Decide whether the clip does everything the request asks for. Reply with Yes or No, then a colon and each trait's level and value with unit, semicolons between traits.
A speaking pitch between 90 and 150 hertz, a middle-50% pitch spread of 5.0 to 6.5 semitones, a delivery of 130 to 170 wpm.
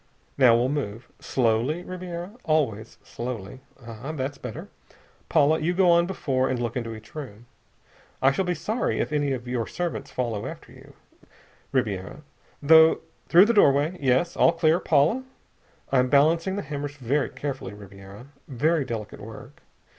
Yes: medium, 140 Hz; wide, 5.5 semitones; average, 150 wpm